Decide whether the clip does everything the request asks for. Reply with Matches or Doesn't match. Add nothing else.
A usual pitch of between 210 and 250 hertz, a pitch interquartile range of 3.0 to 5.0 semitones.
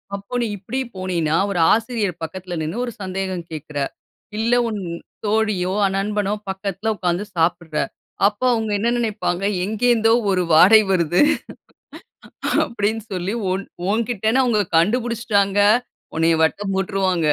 Doesn't match